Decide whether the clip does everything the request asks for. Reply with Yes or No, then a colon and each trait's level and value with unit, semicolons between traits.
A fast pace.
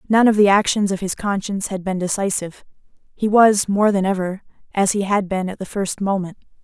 Yes: fast, 210 wpm